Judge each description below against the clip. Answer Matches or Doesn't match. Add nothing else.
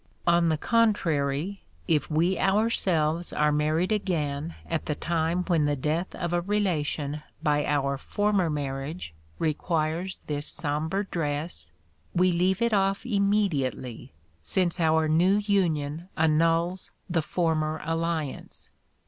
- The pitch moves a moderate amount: Matches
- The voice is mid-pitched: Matches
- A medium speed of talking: Doesn't match